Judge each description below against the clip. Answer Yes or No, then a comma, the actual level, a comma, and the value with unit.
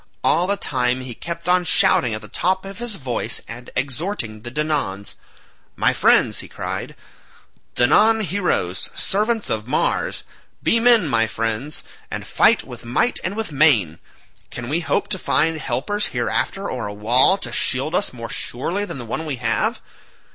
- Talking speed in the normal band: Yes, average, 170 wpm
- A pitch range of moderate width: No, wide, 8.2 semitones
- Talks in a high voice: No, medium, 145 Hz